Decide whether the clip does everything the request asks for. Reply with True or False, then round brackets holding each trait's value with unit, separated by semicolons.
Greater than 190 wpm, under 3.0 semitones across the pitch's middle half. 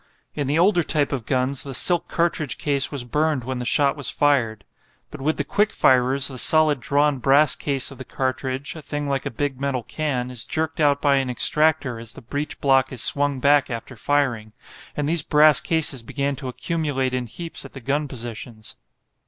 True (200 wpm; 2.6 semitones)